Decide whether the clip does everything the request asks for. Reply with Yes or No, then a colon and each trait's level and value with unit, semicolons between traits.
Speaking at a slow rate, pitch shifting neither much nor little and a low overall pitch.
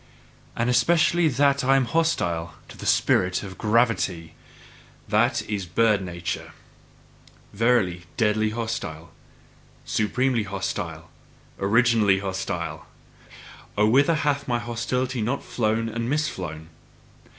Yes: slow, 105 wpm; average, 4.5 semitones; low, 115 Hz